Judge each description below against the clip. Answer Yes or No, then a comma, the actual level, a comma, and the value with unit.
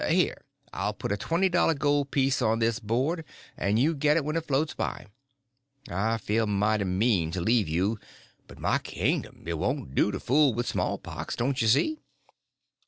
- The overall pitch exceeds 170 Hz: No, low, 115 Hz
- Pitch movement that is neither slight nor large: No, wide, 5.9 semitones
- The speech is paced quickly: No, average, 185 wpm